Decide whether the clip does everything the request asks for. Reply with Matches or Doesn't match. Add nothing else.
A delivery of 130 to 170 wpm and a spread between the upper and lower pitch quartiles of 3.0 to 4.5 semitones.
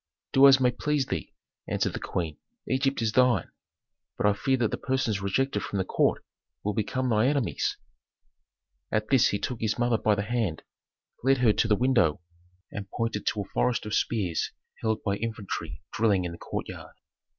Doesn't match